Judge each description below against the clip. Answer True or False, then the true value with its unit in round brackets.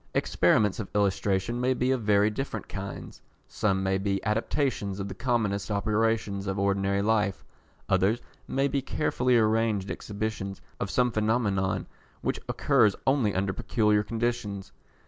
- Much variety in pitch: False (2.7 semitones)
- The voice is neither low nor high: False (105 Hz)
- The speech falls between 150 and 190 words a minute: False (140 wpm)